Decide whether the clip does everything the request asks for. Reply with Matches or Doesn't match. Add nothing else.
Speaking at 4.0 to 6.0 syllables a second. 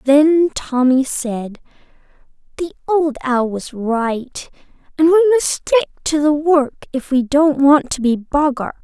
Doesn't match